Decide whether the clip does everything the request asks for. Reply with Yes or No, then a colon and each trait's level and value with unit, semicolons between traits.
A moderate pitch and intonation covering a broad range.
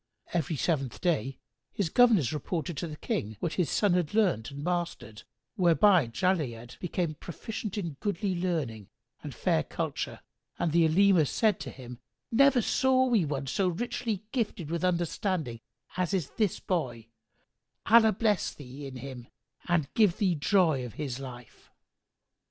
Yes: medium, 170 Hz; wide, 6.5 semitones